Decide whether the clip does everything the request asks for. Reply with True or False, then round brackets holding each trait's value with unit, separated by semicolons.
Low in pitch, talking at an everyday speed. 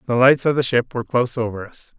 False (125 Hz; 270 wpm)